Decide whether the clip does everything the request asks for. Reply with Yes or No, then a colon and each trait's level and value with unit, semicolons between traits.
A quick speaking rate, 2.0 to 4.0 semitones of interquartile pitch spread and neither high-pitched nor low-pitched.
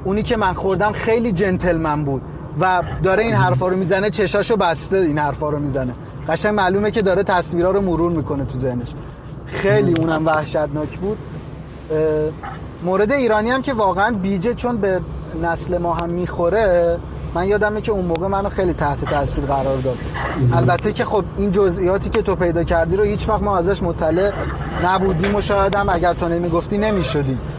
No: fast, 170 wpm; average, 4.5 semitones; medium, 175 Hz